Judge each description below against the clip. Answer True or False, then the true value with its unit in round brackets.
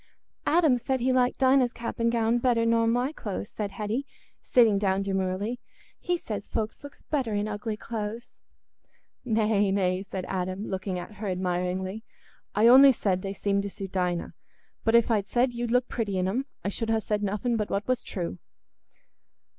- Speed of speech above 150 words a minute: True (180 wpm)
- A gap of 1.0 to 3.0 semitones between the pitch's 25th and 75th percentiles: False (3.6 semitones)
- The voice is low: False (215 Hz)